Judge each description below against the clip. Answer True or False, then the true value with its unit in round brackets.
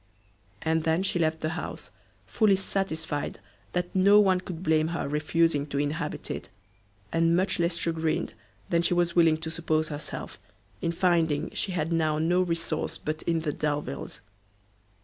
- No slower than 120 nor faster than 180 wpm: True (160 wpm)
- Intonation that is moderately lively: False (1.9 semitones)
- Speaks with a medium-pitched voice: True (165 Hz)